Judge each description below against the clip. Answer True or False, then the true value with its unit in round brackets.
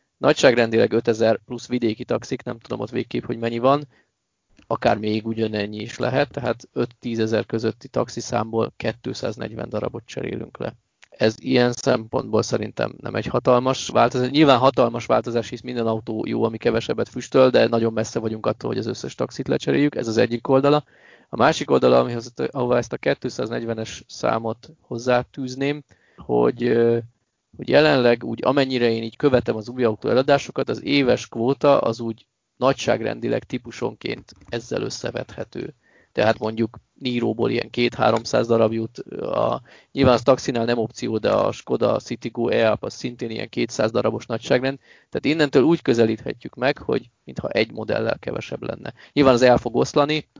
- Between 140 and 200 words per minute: True (155 wpm)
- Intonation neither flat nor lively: False (2.3 semitones)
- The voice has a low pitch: True (120 Hz)